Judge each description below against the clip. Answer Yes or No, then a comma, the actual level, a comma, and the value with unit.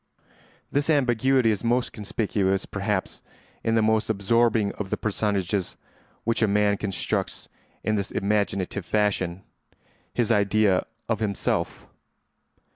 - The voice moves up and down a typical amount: No, narrow, 2.3 semitones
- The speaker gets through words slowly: Yes, slow, 115 wpm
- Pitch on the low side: Yes, low, 105 Hz